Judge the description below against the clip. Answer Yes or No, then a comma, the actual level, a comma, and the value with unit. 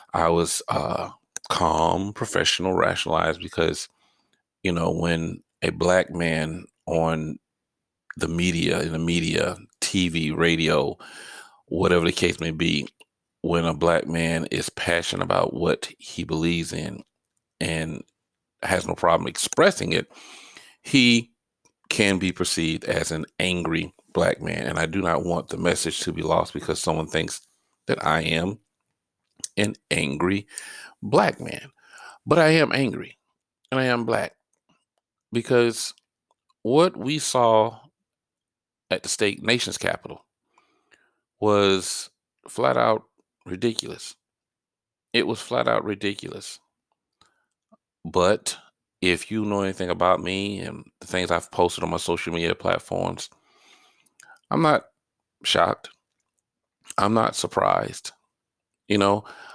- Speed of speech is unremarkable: No, slow, 125 wpm